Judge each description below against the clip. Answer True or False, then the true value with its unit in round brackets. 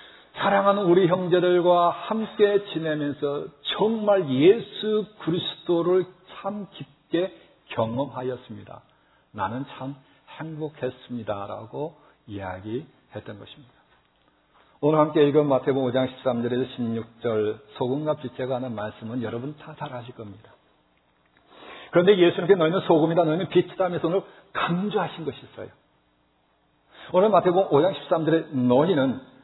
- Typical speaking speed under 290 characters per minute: True (275 characters per minute)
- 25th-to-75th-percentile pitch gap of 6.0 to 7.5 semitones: True (6.3 semitones)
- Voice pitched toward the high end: False (150 Hz)